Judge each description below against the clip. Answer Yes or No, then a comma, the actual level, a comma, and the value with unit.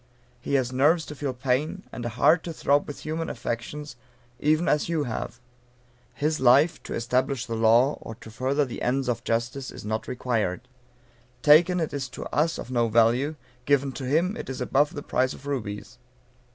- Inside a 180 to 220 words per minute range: Yes, average, 190 wpm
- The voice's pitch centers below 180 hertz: Yes, low, 135 Hz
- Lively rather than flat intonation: No, average, 3.8 semitones